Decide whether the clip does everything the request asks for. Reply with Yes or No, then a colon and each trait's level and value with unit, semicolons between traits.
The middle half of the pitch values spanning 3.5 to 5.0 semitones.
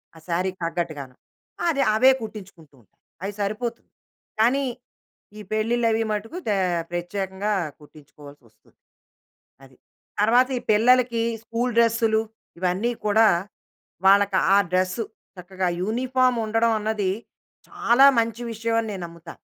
Yes: average, 3.9 semitones